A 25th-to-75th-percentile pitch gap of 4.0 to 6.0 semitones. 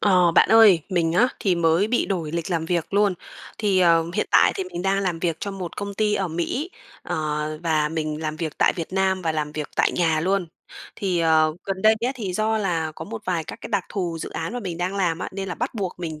No: average, 3.4 semitones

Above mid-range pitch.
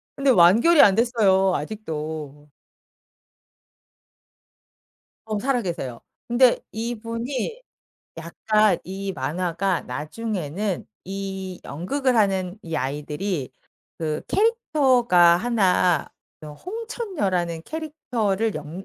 Yes: high, 195 Hz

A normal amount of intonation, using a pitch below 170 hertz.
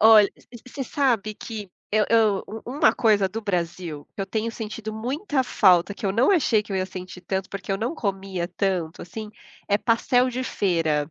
No: average, 3.4 semitones; high, 210 Hz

